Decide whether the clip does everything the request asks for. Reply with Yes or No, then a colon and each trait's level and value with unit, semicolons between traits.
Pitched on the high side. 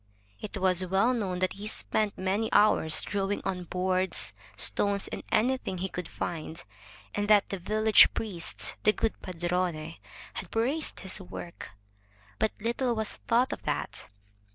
Yes: high, 195 Hz